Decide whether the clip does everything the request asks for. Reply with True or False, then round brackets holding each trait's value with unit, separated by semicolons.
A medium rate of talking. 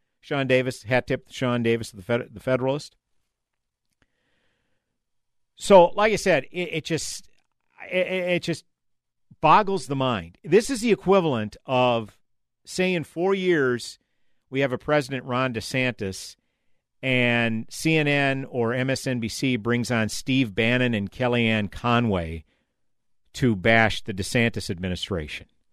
False (130 wpm)